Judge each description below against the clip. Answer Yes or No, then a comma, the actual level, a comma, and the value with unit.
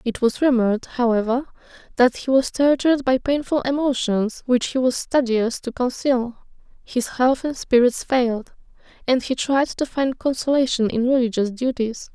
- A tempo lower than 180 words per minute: Yes, average, 155 wpm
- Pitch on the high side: Yes, very high, 250 Hz